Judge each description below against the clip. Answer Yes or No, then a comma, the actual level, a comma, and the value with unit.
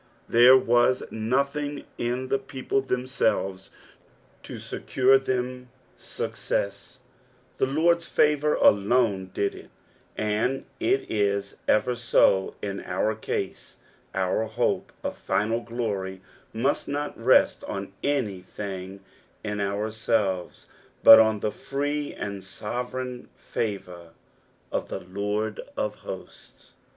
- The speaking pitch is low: Yes, low, 110 Hz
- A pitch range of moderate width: Yes, average, 4.5 semitones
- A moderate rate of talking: No, slow, 110 wpm